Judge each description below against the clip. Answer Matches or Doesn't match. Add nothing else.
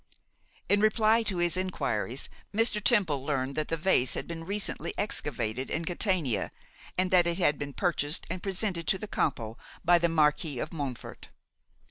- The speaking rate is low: Doesn't match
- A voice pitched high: Doesn't match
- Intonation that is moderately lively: Matches